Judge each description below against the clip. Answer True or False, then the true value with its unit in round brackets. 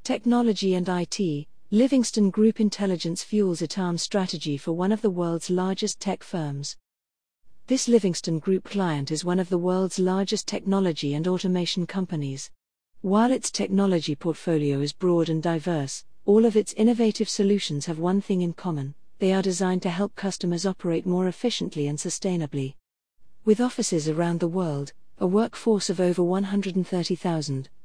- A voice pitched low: False (185 Hz)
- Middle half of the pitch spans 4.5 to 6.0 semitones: False (3.4 semitones)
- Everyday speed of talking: True (150 wpm)